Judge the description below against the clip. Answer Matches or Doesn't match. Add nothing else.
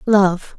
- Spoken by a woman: Matches